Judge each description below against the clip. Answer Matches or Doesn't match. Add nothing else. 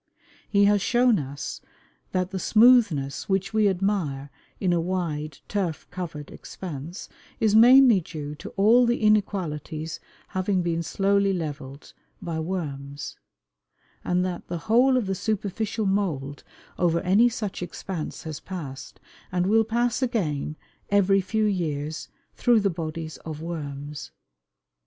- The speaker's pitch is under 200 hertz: Matches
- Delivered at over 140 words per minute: Doesn't match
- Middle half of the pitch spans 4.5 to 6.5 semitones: Matches